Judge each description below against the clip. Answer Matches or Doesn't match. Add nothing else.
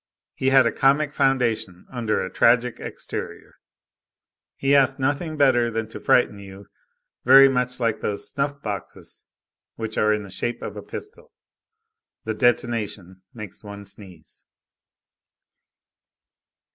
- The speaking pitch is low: Matches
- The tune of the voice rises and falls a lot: Doesn't match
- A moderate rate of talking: Doesn't match